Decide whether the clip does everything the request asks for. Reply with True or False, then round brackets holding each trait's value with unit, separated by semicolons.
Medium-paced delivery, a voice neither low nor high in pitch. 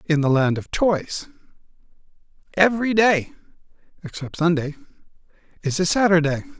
False (110 wpm; 175 Hz)